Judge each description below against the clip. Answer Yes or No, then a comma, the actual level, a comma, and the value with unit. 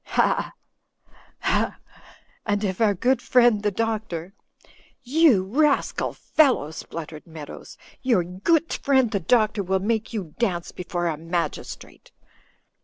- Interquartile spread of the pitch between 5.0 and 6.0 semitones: Yes, wide, 5.5 semitones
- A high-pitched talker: Yes, high, 205 Hz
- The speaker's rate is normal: No, slow, 130 wpm